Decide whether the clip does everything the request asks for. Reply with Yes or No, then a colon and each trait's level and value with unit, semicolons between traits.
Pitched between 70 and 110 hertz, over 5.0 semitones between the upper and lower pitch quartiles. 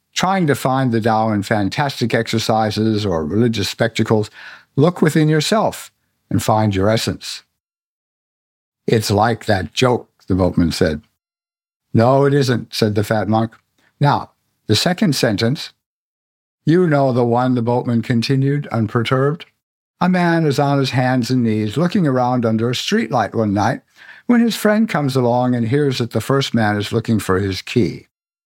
No: low, 125 Hz; wide, 5.4 semitones